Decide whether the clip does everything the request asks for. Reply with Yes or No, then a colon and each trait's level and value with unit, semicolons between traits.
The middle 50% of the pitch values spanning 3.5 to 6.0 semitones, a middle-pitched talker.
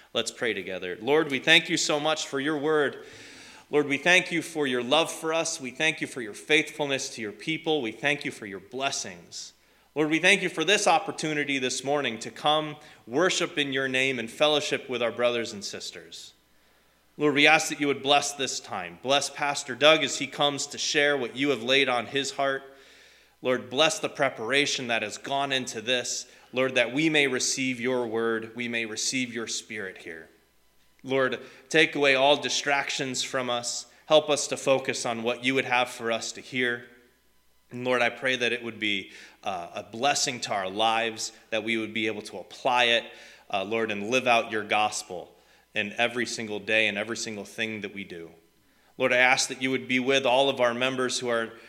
No: average, 3.9 semitones; low, 130 Hz